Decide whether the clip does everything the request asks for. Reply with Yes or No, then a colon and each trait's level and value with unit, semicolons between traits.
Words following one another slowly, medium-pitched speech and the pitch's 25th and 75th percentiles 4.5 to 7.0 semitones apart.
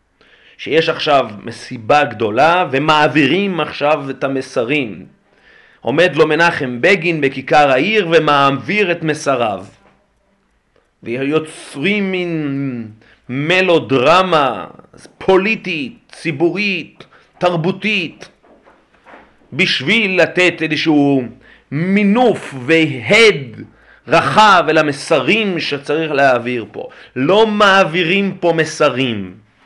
Yes: slow, 75 wpm; medium, 155 Hz; average, 5.1 semitones